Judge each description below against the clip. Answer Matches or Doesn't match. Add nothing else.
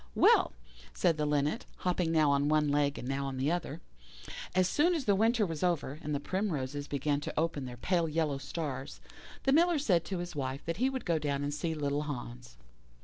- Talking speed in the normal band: Doesn't match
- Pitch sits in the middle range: Matches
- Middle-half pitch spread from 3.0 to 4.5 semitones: Matches